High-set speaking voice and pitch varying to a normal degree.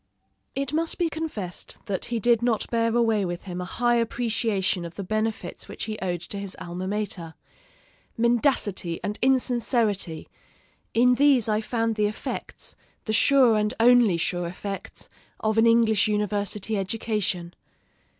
Yes: high, 215 Hz; average, 3.4 semitones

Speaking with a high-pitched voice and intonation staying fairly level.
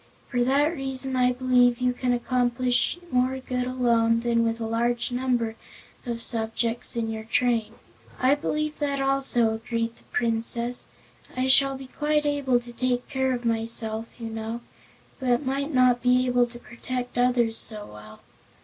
Yes: high, 245 Hz; narrow, 2.0 semitones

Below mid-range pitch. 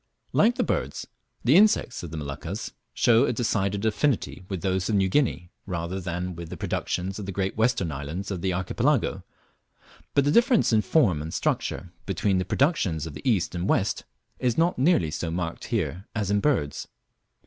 Yes: very low, 95 Hz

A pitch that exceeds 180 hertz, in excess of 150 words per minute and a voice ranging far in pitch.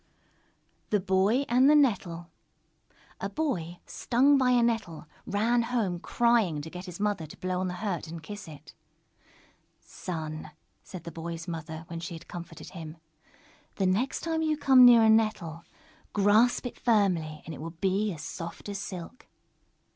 Yes: high, 190 Hz; average, 170 wpm; wide, 5.8 semitones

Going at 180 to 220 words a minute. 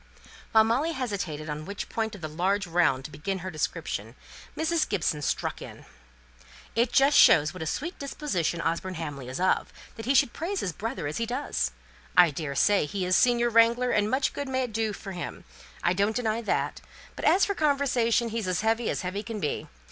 Yes: average, 200 wpm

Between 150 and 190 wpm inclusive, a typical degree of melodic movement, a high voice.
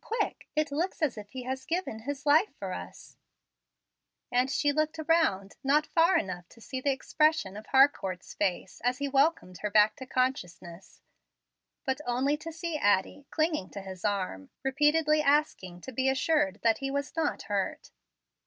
No: average, 170 wpm; wide, 6.8 semitones; very high, 265 Hz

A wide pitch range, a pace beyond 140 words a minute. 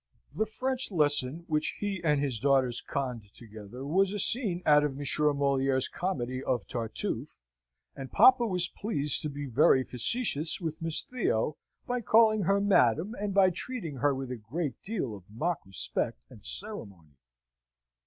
Yes: wide, 7.1 semitones; average, 160 wpm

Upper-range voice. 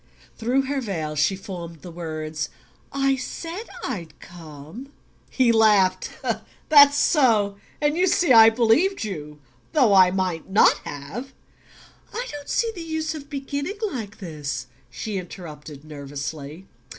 Yes: high, 205 Hz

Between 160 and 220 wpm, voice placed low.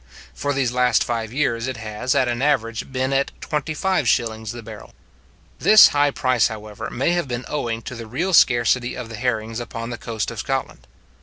Yes: average, 200 wpm; low, 120 Hz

